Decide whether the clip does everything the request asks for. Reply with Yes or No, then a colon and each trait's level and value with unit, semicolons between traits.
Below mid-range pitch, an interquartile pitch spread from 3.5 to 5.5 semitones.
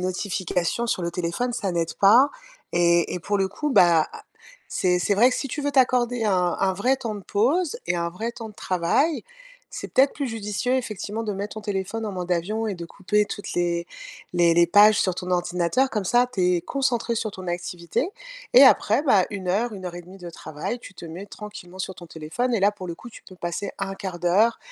No: high, 195 Hz; average, 4.5 semitones